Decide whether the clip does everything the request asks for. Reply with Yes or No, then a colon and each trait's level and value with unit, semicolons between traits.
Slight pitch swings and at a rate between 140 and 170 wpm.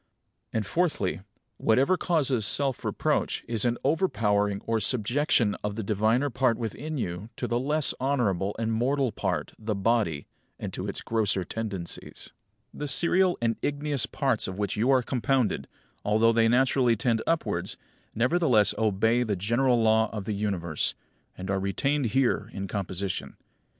No: average, 4.4 semitones; average, 155 wpm